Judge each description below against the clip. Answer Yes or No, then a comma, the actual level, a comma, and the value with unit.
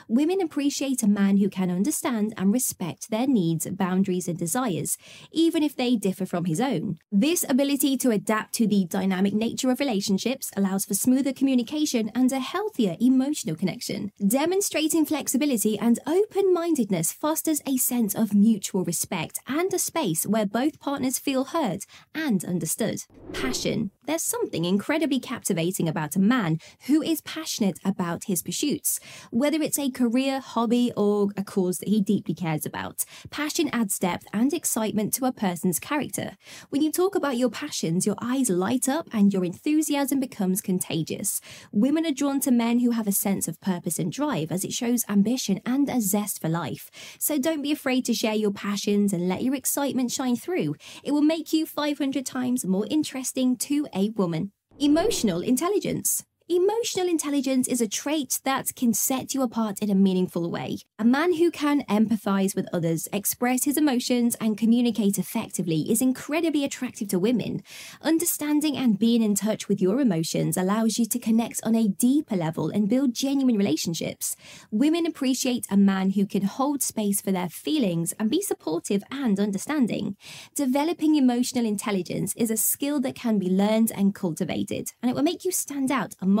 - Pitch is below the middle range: No, high, 235 Hz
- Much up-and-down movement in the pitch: Yes, wide, 6.1 semitones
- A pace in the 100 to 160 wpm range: No, average, 175 wpm